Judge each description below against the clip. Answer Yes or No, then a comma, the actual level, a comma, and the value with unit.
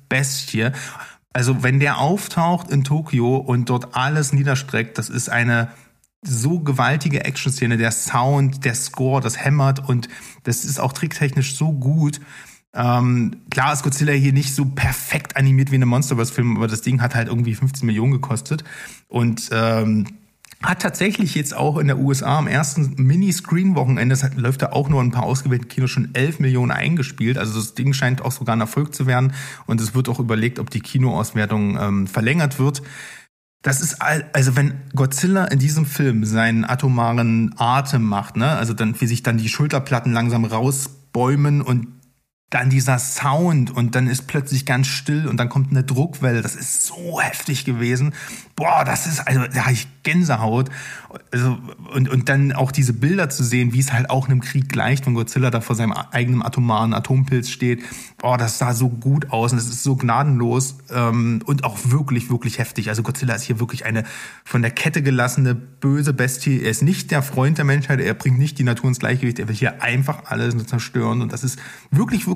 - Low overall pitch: Yes, low, 130 Hz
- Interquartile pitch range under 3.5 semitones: Yes, average, 2.7 semitones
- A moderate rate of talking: No, fast, 195 wpm